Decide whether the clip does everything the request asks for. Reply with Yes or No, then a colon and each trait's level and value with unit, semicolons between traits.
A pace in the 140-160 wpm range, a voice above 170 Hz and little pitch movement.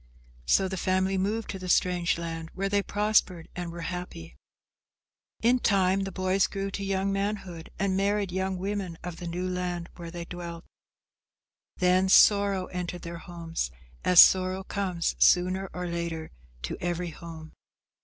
Yes: average, 155 wpm; medium, 185 Hz; narrow, 2.1 semitones